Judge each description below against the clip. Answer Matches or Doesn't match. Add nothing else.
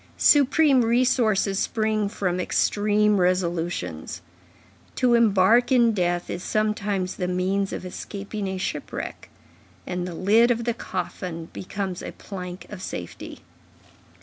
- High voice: Matches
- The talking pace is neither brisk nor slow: Doesn't match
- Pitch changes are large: Doesn't match